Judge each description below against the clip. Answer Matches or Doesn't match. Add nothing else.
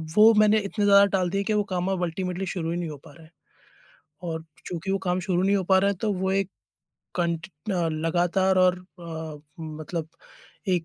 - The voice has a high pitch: Doesn't match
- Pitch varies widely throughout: Doesn't match